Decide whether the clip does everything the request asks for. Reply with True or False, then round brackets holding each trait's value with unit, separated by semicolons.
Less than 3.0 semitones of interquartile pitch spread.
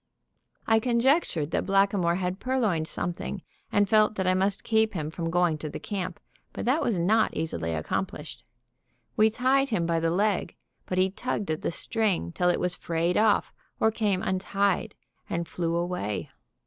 False (4.2 semitones)